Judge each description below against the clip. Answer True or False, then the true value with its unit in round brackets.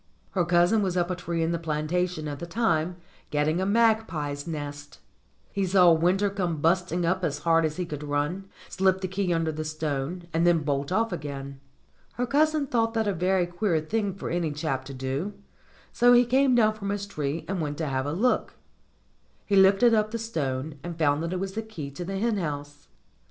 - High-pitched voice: False (175 Hz)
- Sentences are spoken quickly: True (210 wpm)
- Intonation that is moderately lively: True (4.6 semitones)